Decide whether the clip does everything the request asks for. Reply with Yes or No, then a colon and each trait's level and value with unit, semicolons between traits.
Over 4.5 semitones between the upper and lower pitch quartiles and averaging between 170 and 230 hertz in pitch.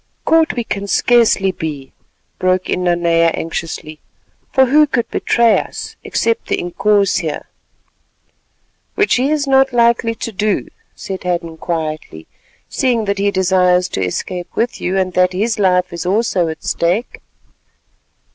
Yes: average, 4.9 semitones; high, 190 Hz